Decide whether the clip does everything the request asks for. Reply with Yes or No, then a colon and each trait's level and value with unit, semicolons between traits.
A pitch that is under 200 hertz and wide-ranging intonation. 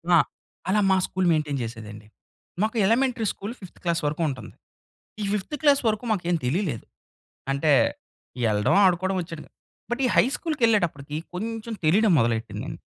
Yes: medium, 185 Hz; wide, 7.2 semitones